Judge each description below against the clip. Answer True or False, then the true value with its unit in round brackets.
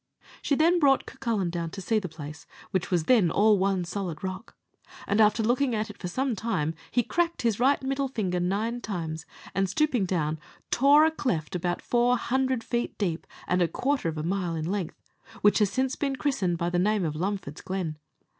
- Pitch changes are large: True (6.0 semitones)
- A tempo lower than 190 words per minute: False (200 wpm)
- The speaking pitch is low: False (200 Hz)